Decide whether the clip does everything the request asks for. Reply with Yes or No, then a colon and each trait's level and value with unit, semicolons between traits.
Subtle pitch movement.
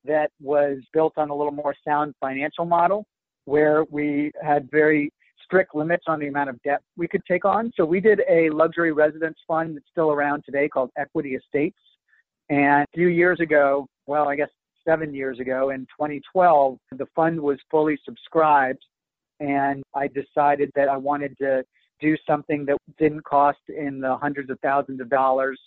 Yes: narrow, 2.2 semitones